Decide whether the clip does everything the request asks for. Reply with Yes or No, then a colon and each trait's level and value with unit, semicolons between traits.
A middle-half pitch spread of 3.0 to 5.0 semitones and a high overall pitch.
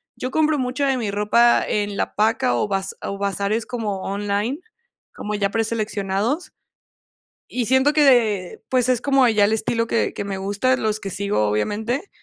Yes: average, 3.9 semitones; high, 220 Hz